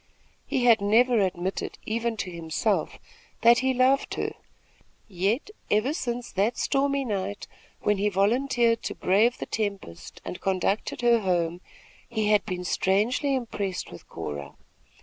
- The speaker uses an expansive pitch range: No, average, 4.3 semitones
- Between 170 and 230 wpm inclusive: No, average, 140 wpm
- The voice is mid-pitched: No, high, 215 Hz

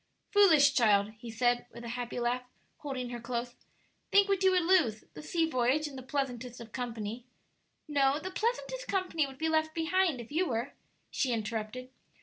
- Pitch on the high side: Yes, very high, 260 Hz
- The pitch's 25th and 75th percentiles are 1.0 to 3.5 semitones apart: No, average, 5.2 semitones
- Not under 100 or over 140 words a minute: No, average, 185 wpm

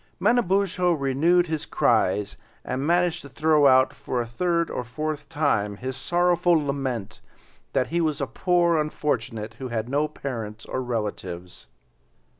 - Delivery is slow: No, average, 145 wpm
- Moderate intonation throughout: No, wide, 5.9 semitones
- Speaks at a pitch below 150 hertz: Yes, medium, 140 Hz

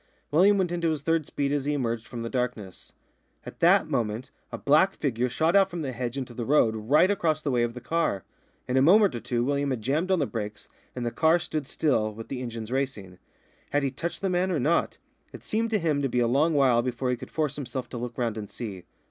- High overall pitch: No, low, 135 Hz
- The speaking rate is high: Yes, fast, 250 wpm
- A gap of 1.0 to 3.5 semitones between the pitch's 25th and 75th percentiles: No, average, 5.1 semitones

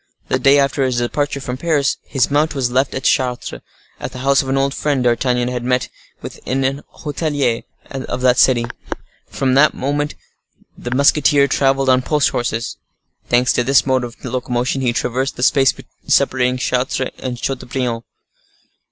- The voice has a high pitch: No, low, 130 Hz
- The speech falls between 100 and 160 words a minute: No, average, 170 wpm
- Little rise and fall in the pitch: Yes, narrow, 1.8 semitones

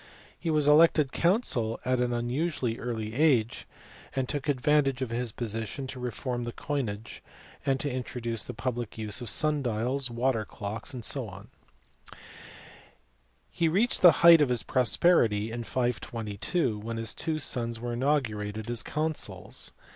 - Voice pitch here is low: Yes, low, 125 Hz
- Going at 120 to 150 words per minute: Yes, average, 145 wpm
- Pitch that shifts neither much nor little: Yes, average, 4.1 semitones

